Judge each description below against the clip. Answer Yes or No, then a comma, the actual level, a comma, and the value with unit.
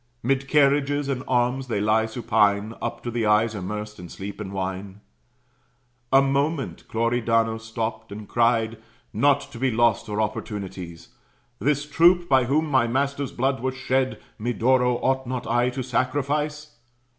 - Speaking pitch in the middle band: No, low, 120 Hz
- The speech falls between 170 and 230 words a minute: No, average, 150 wpm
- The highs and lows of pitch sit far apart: No, average, 3.7 semitones